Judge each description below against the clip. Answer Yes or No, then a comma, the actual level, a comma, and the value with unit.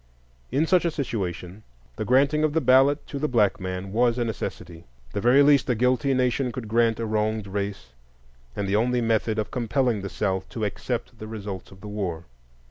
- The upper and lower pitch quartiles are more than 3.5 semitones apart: Yes, average, 4.1 semitones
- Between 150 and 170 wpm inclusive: No, average, 200 wpm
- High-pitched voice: No, low, 115 Hz